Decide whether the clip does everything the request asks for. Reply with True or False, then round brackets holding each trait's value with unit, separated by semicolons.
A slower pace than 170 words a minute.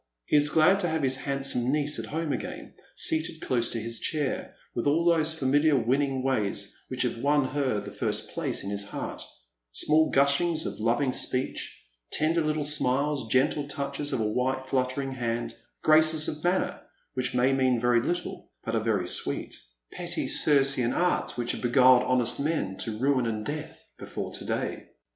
False (180 wpm)